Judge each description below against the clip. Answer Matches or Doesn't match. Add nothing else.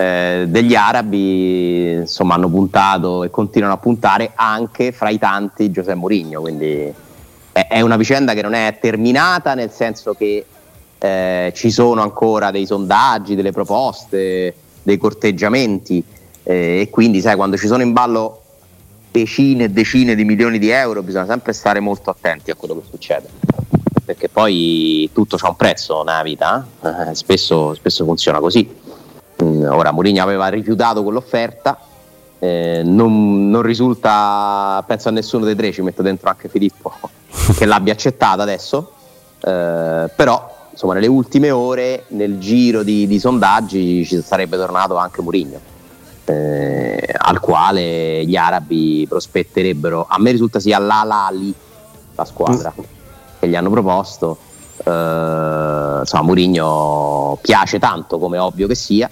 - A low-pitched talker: Matches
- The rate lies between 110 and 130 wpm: Doesn't match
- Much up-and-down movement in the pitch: Doesn't match